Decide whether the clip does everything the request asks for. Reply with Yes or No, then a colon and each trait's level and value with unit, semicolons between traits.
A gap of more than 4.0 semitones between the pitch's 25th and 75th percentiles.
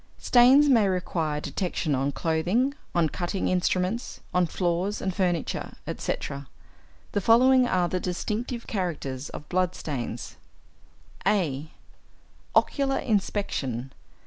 Yes: average, 5.1 semitones